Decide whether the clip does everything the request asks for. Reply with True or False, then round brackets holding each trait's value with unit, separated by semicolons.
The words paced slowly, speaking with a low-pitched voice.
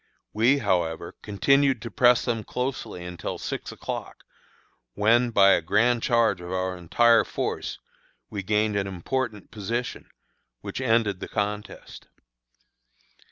True (125 wpm; 105 Hz)